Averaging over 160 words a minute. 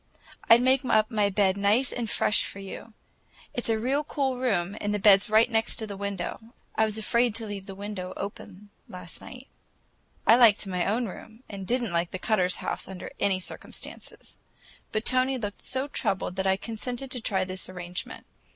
Yes: average, 195 wpm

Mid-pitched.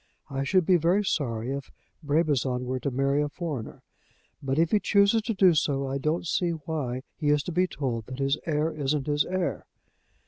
Yes: medium, 150 Hz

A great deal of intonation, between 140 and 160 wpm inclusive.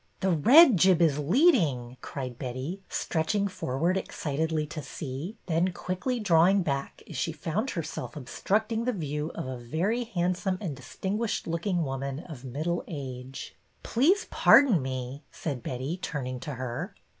Yes: wide, 6.0 semitones; average, 155 wpm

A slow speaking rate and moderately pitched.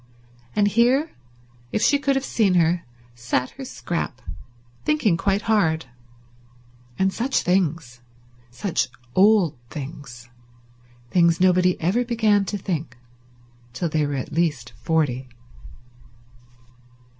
Yes: slow, 110 wpm; medium, 180 Hz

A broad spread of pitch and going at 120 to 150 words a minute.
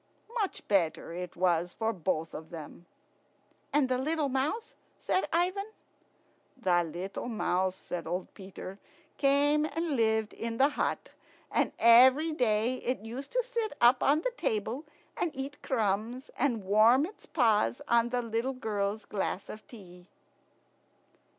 Yes: wide, 6.3 semitones; average, 145 wpm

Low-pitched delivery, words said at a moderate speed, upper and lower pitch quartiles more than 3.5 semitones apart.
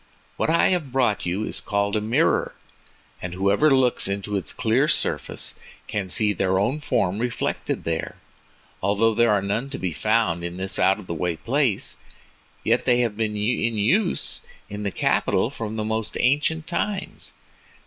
Yes: low, 110 Hz; average, 170 wpm; average, 4.1 semitones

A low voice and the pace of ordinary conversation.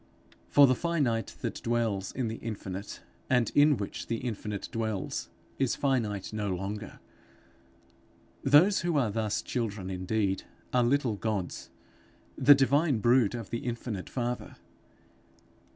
No: low, 115 Hz; slow, 130 wpm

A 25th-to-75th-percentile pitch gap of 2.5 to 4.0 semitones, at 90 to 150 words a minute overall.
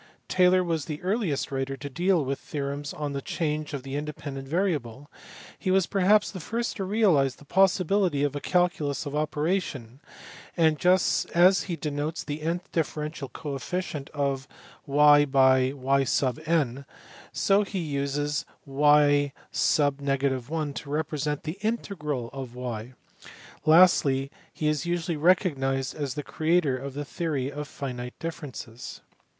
Yes: average, 3.7 semitones; average, 145 wpm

